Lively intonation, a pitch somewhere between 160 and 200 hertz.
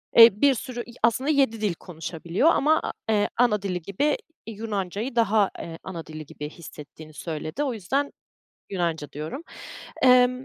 No: wide, 6.8 semitones; high, 210 Hz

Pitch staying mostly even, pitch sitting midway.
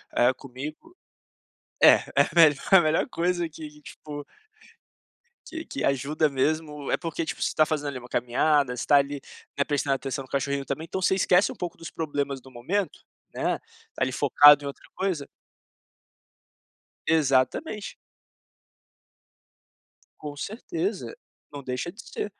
No: average, 3.4 semitones; medium, 150 Hz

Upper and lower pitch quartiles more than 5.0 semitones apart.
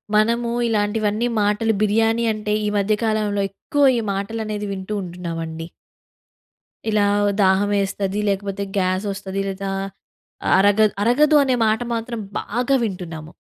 No: narrow, 2.4 semitones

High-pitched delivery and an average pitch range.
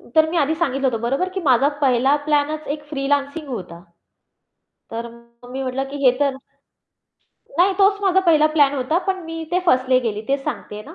Yes: very high, 280 Hz; average, 4.0 semitones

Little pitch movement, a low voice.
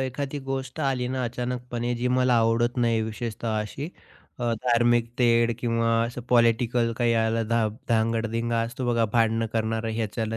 Yes: narrow, 1.4 semitones; low, 115 Hz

